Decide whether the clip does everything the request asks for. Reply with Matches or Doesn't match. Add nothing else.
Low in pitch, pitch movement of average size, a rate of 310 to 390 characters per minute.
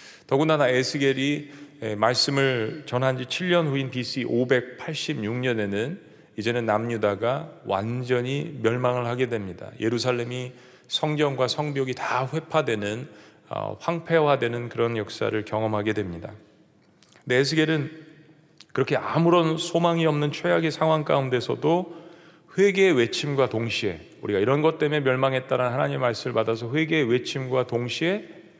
Doesn't match